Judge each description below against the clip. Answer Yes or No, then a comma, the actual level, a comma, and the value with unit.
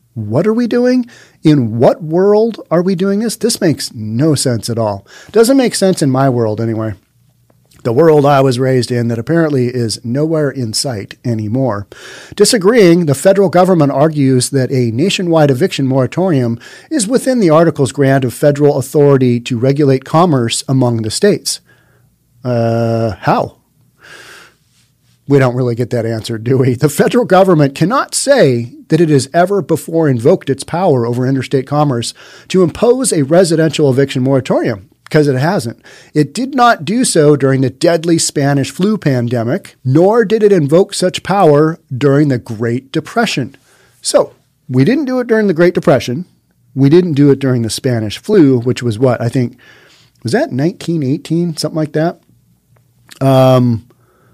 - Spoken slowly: No, average, 160 wpm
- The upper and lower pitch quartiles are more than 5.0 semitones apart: Yes, wide, 5.5 semitones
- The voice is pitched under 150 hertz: Yes, medium, 140 Hz